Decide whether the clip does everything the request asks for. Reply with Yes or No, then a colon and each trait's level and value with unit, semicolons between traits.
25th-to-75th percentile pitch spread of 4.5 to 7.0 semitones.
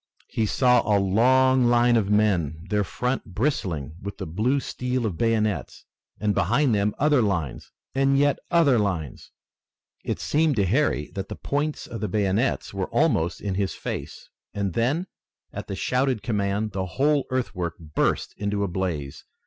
Yes: average, 5.2 semitones